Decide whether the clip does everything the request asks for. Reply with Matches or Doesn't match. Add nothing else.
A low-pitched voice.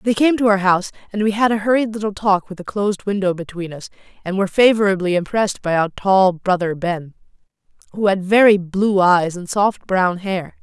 Doesn't match